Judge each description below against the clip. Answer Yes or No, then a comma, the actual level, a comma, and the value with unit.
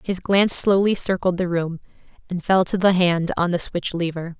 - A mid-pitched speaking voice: Yes, medium, 180 Hz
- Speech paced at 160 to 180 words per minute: No, fast, 205 wpm